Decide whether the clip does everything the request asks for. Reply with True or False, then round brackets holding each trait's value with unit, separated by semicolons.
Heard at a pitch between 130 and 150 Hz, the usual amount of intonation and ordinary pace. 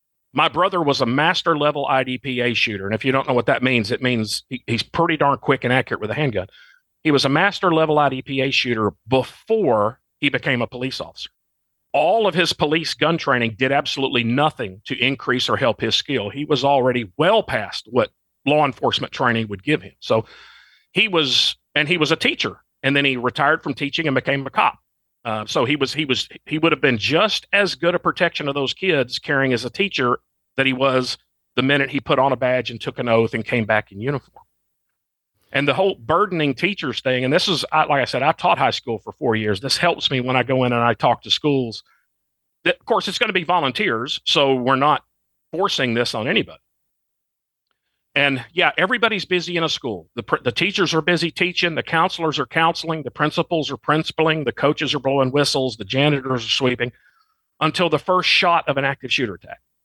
False (140 Hz; 4.3 semitones; 210 wpm)